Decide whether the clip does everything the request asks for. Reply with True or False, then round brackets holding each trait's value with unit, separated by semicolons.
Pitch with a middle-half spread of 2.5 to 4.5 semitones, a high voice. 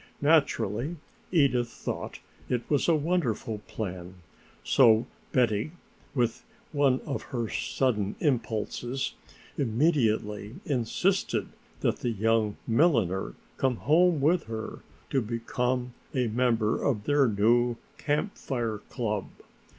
False (4.2 semitones; 120 Hz)